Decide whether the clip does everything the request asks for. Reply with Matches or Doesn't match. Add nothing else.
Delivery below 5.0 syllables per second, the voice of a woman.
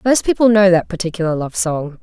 Doesn't match